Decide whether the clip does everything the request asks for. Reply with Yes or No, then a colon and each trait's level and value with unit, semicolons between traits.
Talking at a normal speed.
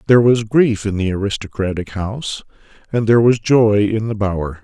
Yes: average, 180 wpm